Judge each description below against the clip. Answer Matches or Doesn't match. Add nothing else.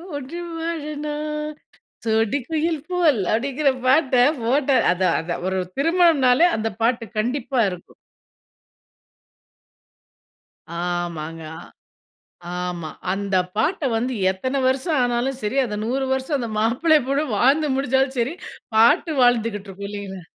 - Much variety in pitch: Matches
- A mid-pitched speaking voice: Doesn't match